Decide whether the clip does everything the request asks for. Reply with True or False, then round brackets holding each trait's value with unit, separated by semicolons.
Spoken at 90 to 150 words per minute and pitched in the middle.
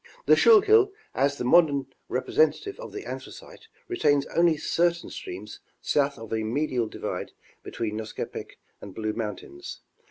True (135 wpm; 145 Hz)